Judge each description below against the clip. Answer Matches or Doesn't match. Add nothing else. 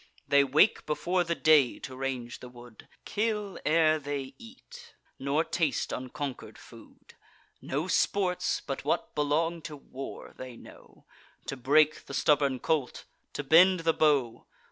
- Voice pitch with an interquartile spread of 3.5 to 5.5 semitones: Matches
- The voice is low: Doesn't match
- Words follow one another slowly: Doesn't match